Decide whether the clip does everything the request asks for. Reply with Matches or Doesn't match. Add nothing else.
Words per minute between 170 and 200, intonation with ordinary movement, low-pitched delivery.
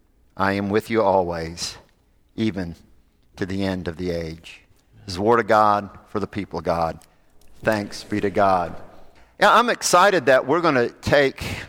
Matches